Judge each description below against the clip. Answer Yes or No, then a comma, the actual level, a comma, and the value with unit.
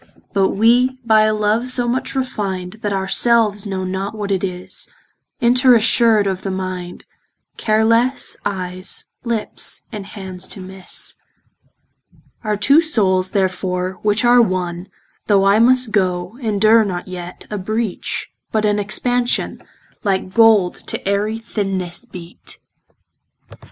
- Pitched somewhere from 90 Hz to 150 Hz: No, high, 205 Hz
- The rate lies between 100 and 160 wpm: Yes, slow, 135 wpm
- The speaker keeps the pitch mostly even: No, average, 3.3 semitones